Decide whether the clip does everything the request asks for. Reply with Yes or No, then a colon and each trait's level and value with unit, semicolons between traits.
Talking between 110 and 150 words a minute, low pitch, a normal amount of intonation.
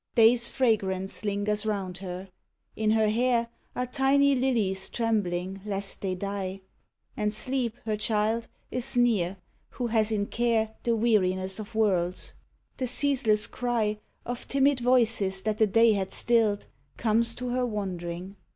No: average, 140 wpm; high, 215 Hz; average, 3.4 semitones